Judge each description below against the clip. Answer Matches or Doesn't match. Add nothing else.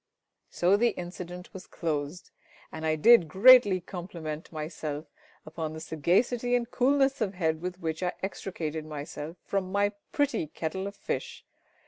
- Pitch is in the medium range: Matches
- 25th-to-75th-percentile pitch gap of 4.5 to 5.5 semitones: Doesn't match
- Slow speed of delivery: Doesn't match